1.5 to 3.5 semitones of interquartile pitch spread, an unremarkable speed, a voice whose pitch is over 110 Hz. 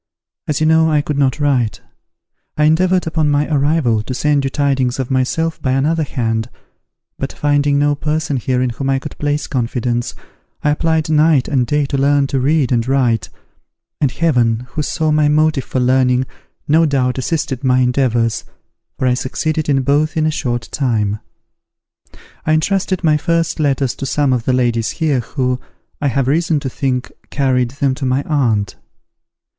Yes: average, 3.2 semitones; average, 175 wpm; medium, 140 Hz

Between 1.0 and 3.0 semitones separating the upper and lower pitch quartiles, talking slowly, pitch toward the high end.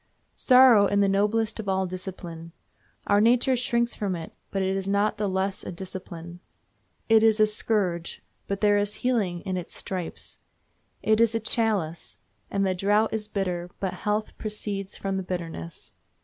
No: narrow, 2.6 semitones; average, 170 wpm; high, 200 Hz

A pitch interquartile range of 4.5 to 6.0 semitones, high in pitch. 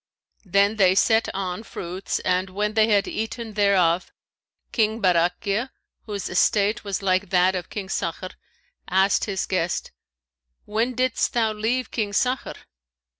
No: average, 3.0 semitones; high, 200 Hz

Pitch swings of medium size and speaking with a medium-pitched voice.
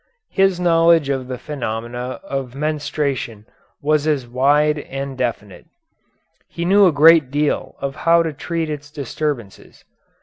Yes: average, 3.3 semitones; medium, 145 Hz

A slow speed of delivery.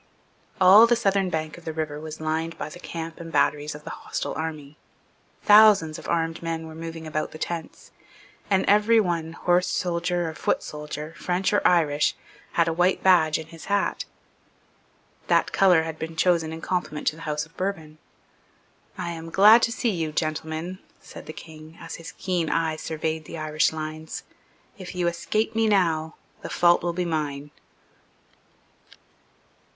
No: average, 175 wpm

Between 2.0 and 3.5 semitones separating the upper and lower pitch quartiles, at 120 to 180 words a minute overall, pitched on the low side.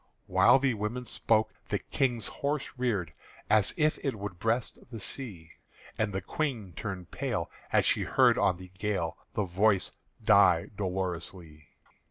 No: average, 5.0 semitones; average, 150 wpm; low, 105 Hz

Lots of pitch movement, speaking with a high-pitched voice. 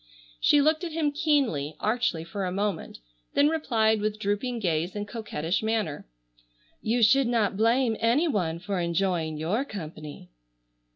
Yes: wide, 6.0 semitones; high, 215 Hz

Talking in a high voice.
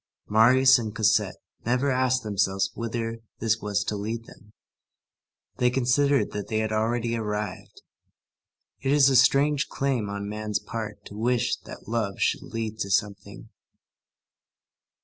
No: low, 115 Hz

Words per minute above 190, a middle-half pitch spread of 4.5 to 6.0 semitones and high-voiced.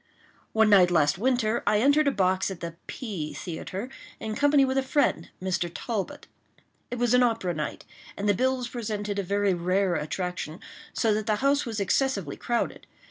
No: average, 180 wpm; average, 5.0 semitones; high, 210 Hz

